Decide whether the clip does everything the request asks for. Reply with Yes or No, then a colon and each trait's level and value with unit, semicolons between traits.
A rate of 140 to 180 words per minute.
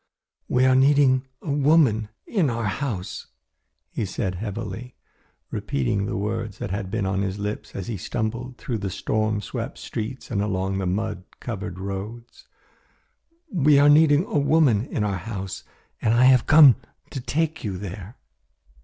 Yes: average, 160 wpm